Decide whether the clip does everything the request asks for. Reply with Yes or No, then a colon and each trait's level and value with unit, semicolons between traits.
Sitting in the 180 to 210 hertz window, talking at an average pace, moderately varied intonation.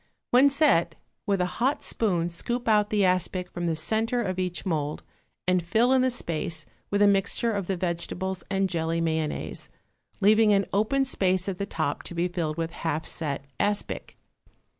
Yes: medium, 185 Hz; average, 180 wpm; average, 4.0 semitones